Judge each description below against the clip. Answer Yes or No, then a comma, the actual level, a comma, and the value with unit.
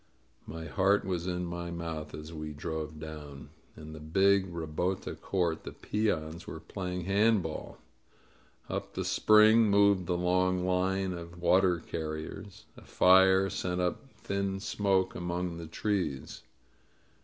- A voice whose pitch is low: Yes, very low, 90 Hz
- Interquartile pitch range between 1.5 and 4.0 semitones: Yes, average, 3.0 semitones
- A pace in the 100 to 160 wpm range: Yes, average, 145 wpm